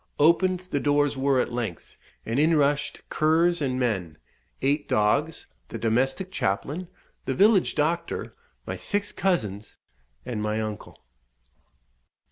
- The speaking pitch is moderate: Yes, medium, 145 Hz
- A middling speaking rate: No, slow, 125 wpm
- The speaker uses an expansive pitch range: Yes, wide, 6.8 semitones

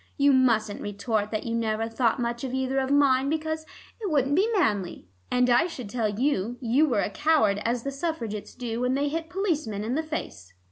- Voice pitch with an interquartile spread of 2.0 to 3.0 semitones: No, average, 4.7 semitones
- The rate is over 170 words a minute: Yes, fast, 205 wpm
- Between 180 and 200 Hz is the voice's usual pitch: No, very high, 250 Hz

